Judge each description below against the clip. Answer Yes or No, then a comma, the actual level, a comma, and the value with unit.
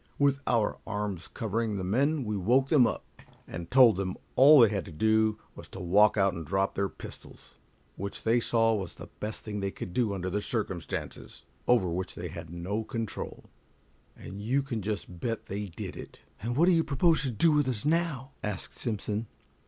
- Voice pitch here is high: No, low, 110 Hz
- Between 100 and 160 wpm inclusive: No, average, 195 wpm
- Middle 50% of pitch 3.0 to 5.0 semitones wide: Yes, average, 4.2 semitones